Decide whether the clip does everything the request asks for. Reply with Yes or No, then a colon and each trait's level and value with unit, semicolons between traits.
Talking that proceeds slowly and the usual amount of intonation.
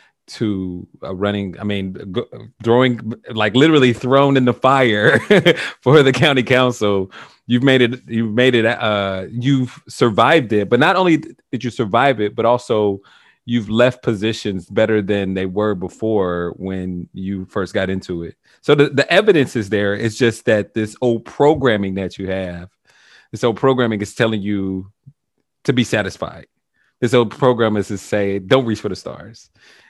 No: average, 165 wpm; average, 3.9 semitones